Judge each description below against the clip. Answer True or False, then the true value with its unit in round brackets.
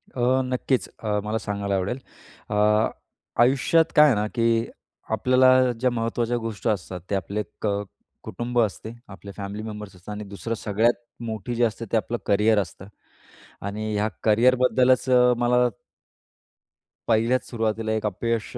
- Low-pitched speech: True (110 Hz)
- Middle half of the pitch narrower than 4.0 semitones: True (2.7 semitones)